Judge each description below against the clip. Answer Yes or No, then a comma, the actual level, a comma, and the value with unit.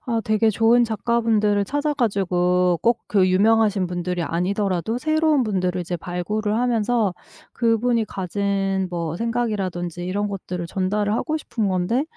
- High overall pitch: Yes, high, 205 Hz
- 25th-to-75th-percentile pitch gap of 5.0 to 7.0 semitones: No, average, 4.0 semitones